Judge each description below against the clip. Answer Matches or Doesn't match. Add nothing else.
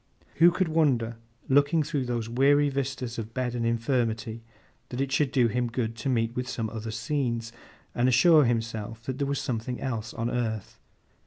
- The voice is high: Doesn't match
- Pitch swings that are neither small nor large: Matches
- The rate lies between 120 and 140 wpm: Doesn't match